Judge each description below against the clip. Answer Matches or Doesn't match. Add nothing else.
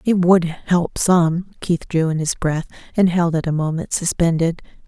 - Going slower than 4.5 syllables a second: Matches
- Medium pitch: Matches